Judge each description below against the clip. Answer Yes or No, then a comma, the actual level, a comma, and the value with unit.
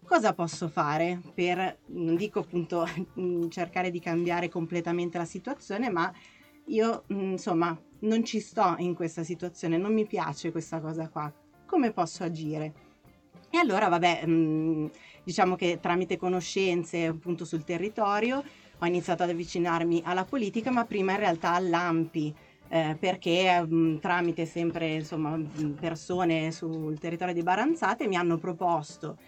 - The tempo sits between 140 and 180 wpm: Yes, average, 145 wpm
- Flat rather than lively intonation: Yes, narrow, 1.9 semitones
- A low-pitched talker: No, medium, 175 Hz